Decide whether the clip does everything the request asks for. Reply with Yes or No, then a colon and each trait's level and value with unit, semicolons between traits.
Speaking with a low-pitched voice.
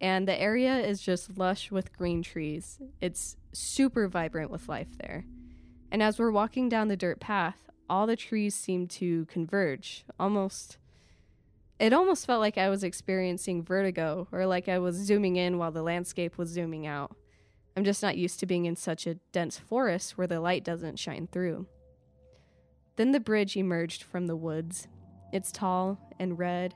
No: medium, 180 Hz